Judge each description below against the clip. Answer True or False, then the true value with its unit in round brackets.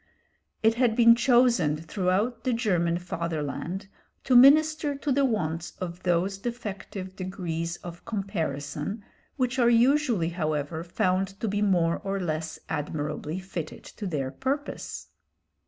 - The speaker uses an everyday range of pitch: False (5.9 semitones)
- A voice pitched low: False (190 Hz)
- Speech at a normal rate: False (130 wpm)